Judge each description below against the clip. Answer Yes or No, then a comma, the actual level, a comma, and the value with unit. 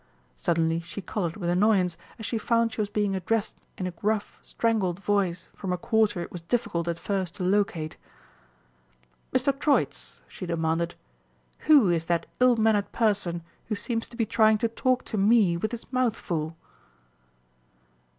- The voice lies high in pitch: Yes, high, 205 Hz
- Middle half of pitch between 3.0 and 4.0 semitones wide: No, average, 4.6 semitones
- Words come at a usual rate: Yes, average, 165 wpm